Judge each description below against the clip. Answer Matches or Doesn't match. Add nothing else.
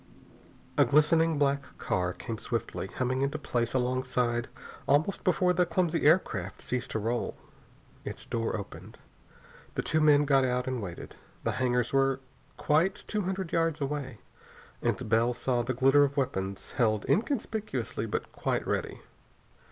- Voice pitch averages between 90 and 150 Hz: Matches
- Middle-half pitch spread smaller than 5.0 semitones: Matches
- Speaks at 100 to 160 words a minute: Matches